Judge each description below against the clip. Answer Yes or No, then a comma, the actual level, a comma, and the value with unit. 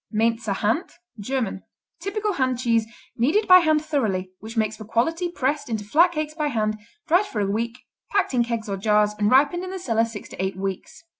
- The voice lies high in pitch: Yes, high, 235 Hz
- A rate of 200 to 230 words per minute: Yes, fast, 205 wpm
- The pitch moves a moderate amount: No, wide, 6.6 semitones